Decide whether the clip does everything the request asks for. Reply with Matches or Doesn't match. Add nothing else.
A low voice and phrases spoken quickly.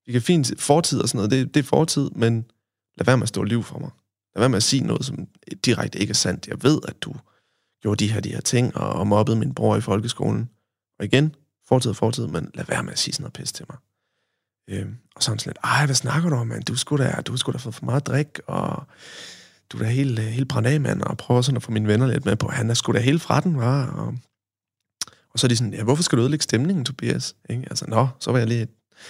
Matches